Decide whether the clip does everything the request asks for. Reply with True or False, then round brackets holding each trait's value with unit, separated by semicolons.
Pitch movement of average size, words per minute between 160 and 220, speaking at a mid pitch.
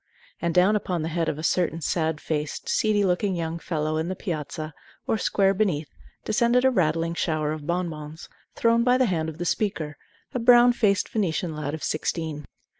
True (4.6 semitones; 190 wpm; 170 Hz)